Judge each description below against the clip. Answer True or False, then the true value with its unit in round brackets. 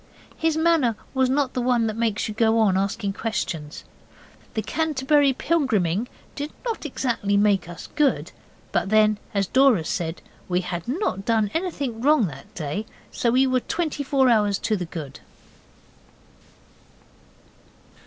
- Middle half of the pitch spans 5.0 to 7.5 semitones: True (5.6 semitones)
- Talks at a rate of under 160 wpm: True (145 wpm)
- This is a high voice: True (225 Hz)